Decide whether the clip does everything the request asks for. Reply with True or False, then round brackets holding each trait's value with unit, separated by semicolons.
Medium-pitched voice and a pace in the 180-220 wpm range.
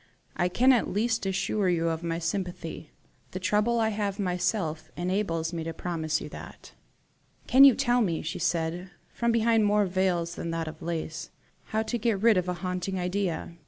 True (180 Hz; 190 wpm)